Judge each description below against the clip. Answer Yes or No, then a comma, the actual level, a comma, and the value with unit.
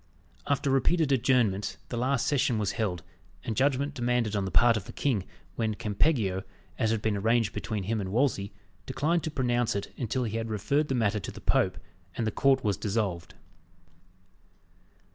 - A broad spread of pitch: No, average, 4.2 semitones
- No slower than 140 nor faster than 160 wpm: No, average, 180 wpm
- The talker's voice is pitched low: Yes, low, 115 Hz